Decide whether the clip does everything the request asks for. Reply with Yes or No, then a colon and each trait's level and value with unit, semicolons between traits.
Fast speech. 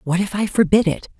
Yes: fast, 250 wpm